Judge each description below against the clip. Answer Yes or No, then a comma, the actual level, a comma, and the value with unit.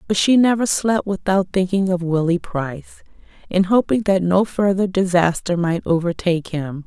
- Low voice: No, medium, 185 Hz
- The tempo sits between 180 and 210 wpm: No, average, 155 wpm